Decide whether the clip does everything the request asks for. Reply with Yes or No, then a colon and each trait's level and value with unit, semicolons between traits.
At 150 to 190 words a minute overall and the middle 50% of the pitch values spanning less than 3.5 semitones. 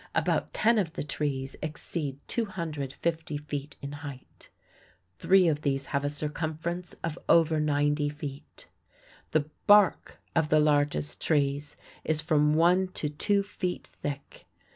No: slow, 135 wpm; narrow, 2.5 semitones